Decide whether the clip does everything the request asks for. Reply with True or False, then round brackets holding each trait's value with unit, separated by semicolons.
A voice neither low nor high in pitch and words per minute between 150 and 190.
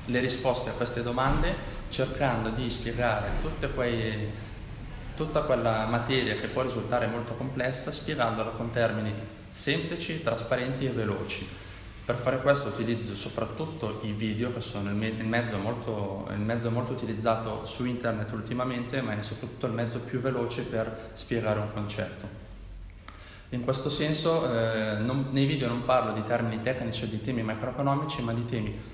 False (115 Hz; 155 wpm)